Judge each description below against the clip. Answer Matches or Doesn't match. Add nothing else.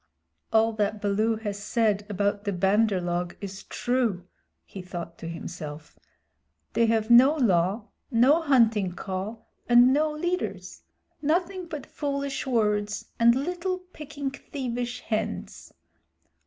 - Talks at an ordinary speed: Doesn't match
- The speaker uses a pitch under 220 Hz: Doesn't match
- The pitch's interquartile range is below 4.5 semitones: Doesn't match